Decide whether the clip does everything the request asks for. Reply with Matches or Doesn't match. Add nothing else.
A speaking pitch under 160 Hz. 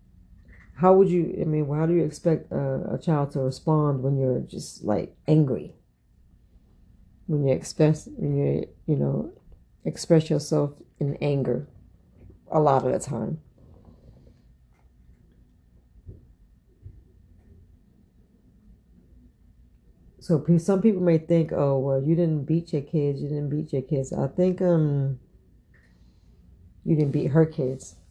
Matches